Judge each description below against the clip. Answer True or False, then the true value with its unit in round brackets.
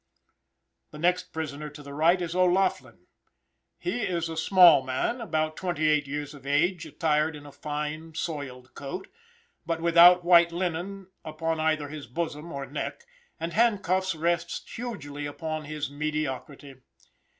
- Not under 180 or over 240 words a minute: False (145 wpm)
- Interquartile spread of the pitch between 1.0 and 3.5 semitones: True (3.0 semitones)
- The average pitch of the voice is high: False (160 Hz)